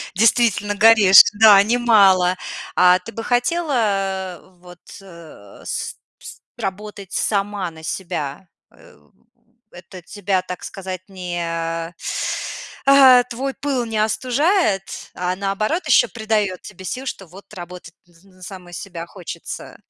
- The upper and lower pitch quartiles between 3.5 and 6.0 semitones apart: Yes, average, 3.8 semitones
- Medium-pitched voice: No, high, 195 Hz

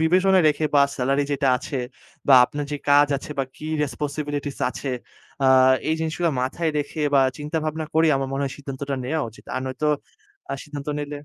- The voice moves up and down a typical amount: No, narrow, 2.2 semitones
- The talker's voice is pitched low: No, medium, 145 Hz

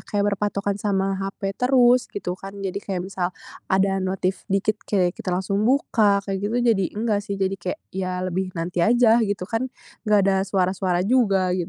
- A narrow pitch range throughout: Yes, narrow, 1.7 semitones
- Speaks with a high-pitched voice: Yes, high, 195 Hz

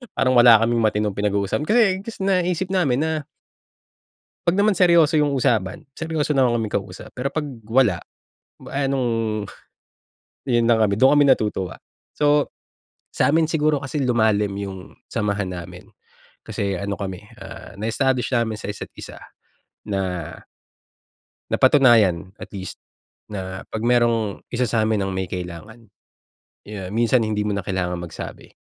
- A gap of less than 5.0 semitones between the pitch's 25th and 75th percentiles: No, wide, 5.4 semitones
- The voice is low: Yes, low, 115 Hz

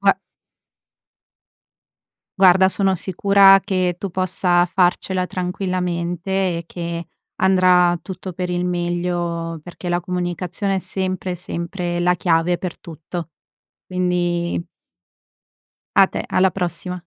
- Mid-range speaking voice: Yes, medium, 180 Hz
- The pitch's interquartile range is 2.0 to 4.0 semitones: No, narrow, 1.2 semitones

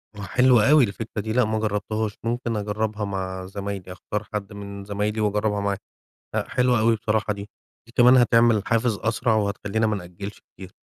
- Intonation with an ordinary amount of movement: No, narrow, 2.0 semitones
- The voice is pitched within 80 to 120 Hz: Yes, low, 105 Hz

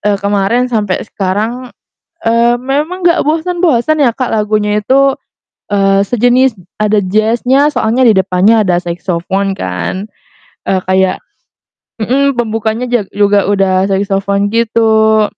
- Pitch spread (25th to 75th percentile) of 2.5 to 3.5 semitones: No, average, 4.0 semitones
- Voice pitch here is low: No, high, 215 Hz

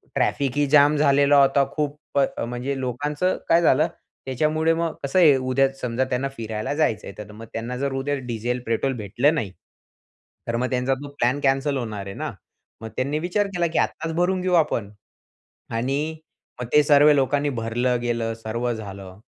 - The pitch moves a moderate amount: Yes, average, 3.8 semitones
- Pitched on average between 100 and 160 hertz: Yes, low, 135 Hz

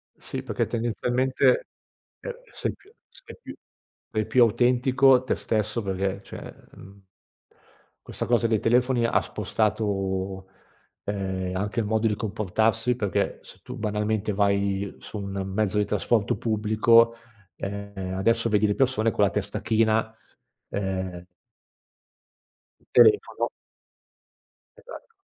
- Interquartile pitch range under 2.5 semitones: No, average, 2.8 semitones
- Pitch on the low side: Yes, low, 110 Hz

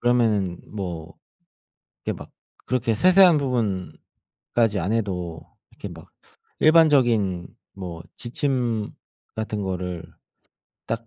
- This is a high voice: No, low, 110 Hz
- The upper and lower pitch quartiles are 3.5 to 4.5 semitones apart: No, average, 5.1 semitones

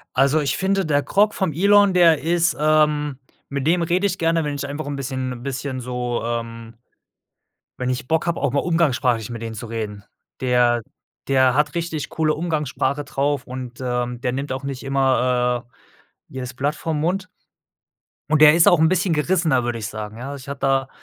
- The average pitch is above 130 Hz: Yes, medium, 140 Hz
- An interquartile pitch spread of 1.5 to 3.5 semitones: No, average, 4.3 semitones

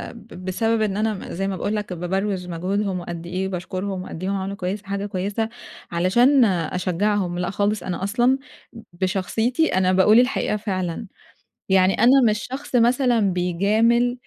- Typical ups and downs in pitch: Yes, average, 3.3 semitones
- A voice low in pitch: No, high, 195 Hz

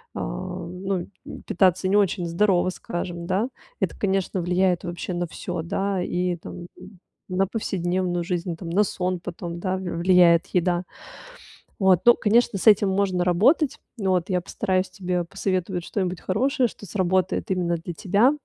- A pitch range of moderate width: No, narrow, 1.8 semitones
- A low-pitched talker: No, medium, 185 Hz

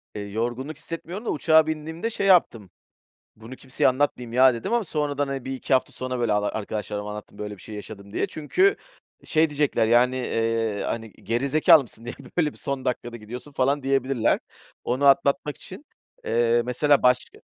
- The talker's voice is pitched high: No, low, 130 Hz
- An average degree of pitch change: Yes, average, 4.3 semitones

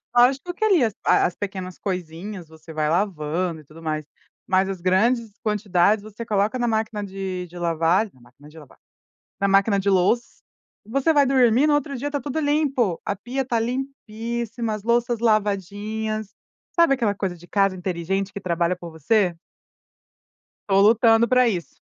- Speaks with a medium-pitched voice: No, high, 205 Hz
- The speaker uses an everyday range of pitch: Yes, average, 4.7 semitones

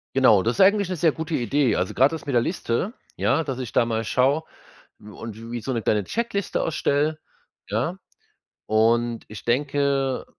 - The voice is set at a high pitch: No, low, 130 Hz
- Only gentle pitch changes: No, average, 5.3 semitones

